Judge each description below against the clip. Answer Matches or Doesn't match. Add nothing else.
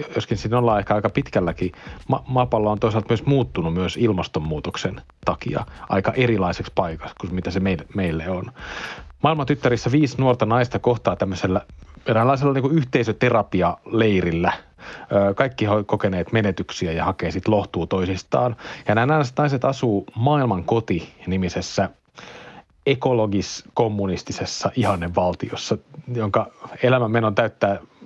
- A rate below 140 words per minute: Matches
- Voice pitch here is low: Matches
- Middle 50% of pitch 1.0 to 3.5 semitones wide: Doesn't match